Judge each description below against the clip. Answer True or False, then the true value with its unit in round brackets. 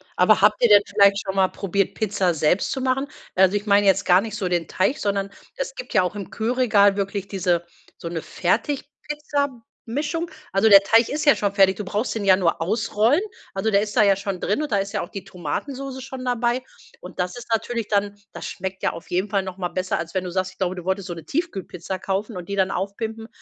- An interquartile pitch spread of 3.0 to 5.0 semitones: True (3.4 semitones)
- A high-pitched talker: True (200 Hz)